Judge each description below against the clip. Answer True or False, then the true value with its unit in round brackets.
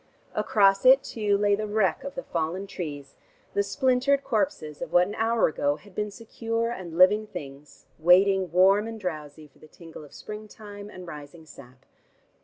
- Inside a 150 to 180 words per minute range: True (175 wpm)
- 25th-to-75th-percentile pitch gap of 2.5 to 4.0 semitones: False (5.2 semitones)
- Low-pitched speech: False (195 Hz)